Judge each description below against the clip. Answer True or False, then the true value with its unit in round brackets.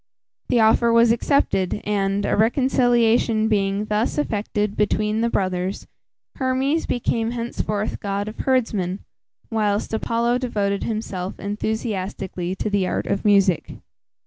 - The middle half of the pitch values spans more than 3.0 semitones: False (2.7 semitones)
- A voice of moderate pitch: False (215 Hz)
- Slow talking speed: True (120 wpm)